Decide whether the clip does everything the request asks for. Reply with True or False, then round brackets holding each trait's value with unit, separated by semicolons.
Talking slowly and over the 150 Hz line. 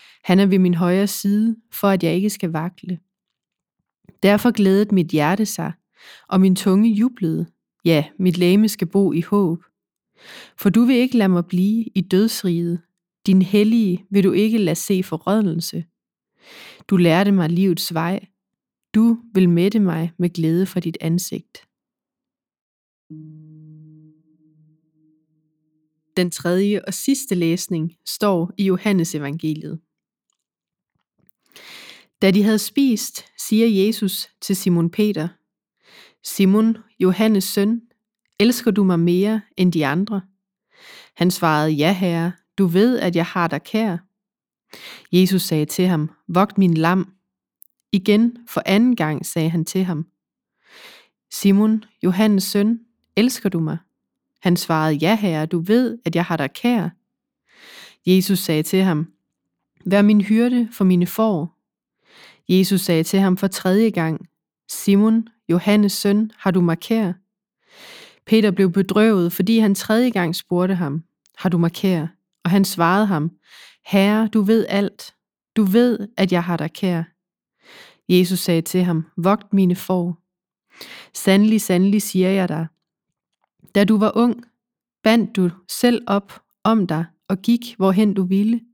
True (140 wpm; 190 Hz)